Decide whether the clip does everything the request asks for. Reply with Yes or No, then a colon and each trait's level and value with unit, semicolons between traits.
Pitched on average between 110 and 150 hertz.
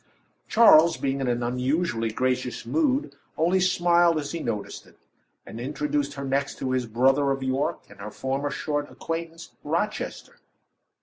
Yes: medium, 140 Hz